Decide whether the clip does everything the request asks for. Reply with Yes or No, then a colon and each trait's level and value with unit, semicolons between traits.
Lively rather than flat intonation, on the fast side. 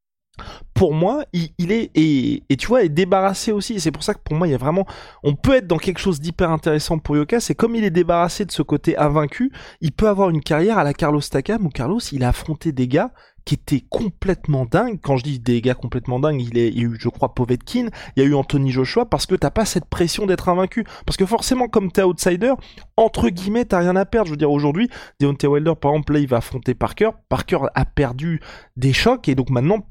Yes: wide, 5.8 semitones; fast, 250 wpm